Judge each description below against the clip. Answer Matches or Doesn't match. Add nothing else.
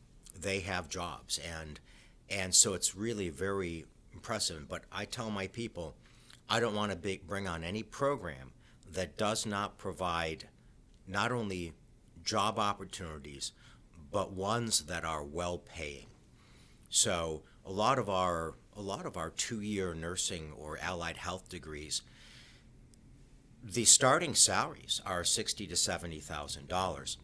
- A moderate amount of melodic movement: Matches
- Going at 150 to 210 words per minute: Doesn't match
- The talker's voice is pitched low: Matches